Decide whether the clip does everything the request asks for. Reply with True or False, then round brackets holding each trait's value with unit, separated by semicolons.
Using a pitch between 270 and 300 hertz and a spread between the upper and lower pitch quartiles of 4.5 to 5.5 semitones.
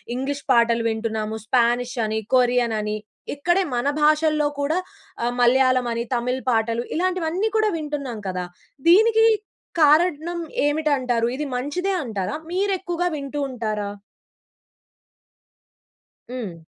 False (260 Hz; 5.2 semitones)